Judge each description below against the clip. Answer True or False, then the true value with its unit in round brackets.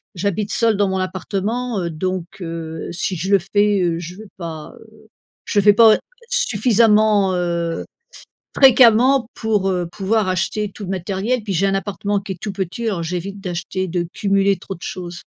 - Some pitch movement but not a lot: True (3.1 semitones)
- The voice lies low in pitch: False (195 Hz)